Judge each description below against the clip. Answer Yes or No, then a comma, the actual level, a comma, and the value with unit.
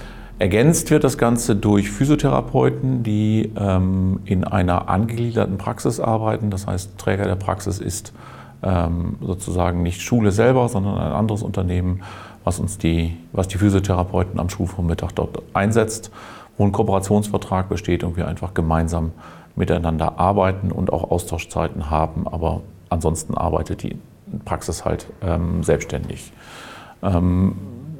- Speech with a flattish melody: No, average, 3.4 semitones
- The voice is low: Yes, very low, 95 Hz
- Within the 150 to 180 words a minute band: No, average, 130 wpm